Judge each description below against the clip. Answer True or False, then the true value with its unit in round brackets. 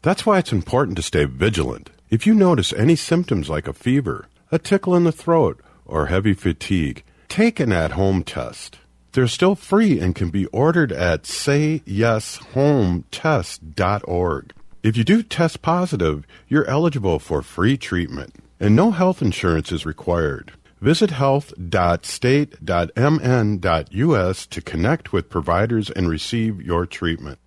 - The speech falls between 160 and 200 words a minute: False (140 wpm)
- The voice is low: True (110 Hz)